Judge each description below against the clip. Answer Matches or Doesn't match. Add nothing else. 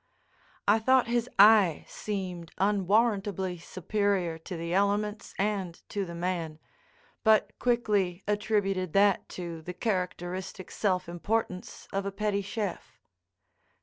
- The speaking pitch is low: Doesn't match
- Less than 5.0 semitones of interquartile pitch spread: Matches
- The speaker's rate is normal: Doesn't match